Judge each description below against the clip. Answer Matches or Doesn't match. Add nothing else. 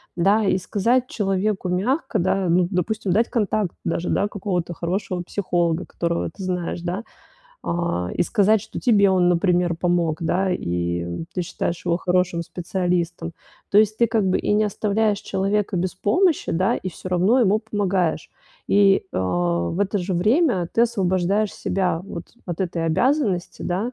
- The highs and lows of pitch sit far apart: Doesn't match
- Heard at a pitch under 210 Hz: Matches